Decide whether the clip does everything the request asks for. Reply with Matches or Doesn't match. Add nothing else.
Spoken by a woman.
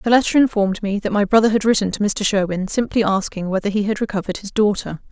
Matches